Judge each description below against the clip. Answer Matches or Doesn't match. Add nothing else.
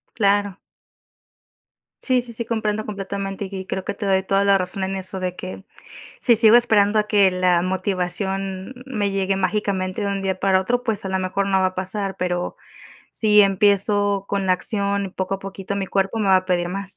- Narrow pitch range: Matches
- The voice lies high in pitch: Matches